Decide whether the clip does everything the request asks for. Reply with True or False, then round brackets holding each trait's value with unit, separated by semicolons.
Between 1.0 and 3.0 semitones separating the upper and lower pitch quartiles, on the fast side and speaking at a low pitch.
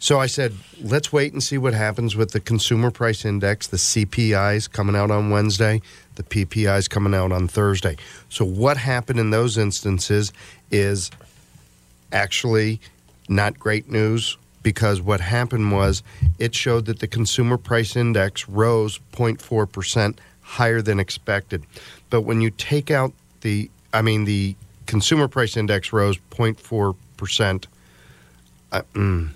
False (2.7 semitones; 140 wpm; 105 Hz)